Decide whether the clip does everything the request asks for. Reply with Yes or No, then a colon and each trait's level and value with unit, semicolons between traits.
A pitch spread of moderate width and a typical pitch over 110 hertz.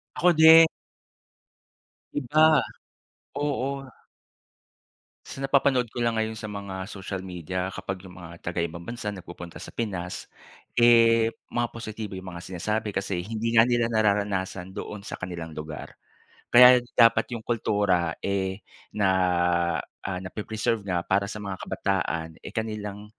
No: average, 3.7 semitones; low, 105 Hz